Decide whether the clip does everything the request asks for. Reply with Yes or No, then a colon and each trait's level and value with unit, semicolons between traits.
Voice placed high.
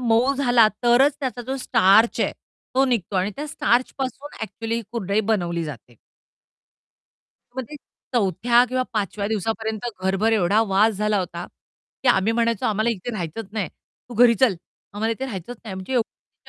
Yes: high, 225 Hz